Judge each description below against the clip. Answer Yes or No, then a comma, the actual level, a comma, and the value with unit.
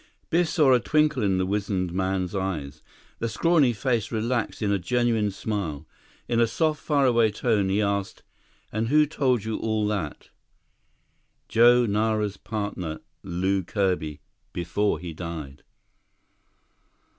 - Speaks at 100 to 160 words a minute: Yes, slow, 135 wpm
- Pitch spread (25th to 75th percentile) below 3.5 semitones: No, average, 4.2 semitones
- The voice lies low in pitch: Yes, low, 105 Hz